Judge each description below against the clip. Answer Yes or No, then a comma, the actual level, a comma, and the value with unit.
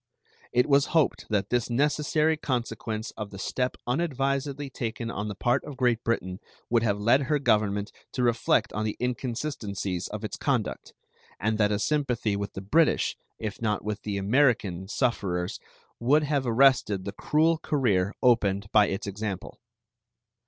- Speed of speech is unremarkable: Yes, average, 160 wpm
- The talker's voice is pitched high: No, low, 115 Hz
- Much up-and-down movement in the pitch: No, average, 4.8 semitones